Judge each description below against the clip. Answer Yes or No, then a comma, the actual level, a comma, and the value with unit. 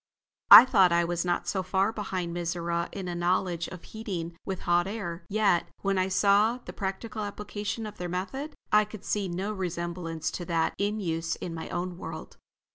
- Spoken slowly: No, average, 190 wpm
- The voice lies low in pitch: No, medium, 185 Hz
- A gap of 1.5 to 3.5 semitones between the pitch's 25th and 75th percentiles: Yes, average, 3.1 semitones